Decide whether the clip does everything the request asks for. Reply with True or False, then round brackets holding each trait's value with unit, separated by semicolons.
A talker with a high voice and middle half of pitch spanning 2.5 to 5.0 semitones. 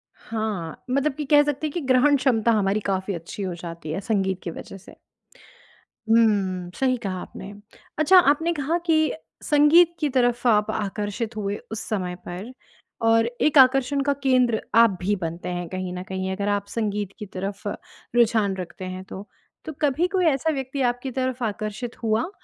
False (220 Hz; 5.6 semitones)